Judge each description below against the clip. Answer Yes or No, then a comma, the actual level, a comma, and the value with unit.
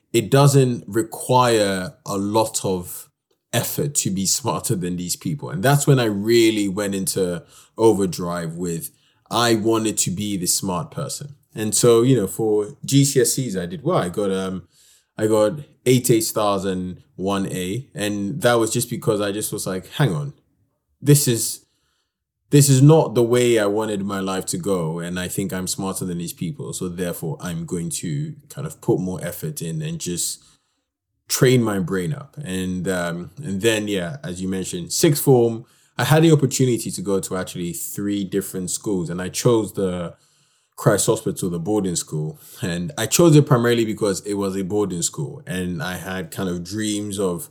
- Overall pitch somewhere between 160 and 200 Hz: No, low, 105 Hz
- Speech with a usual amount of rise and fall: No, wide, 6.1 semitones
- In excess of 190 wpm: No, average, 185 wpm